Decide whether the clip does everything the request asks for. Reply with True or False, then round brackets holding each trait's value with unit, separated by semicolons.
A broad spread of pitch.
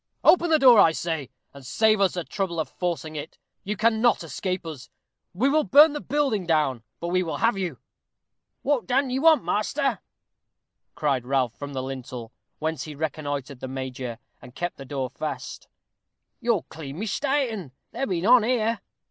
True (8.7 semitones)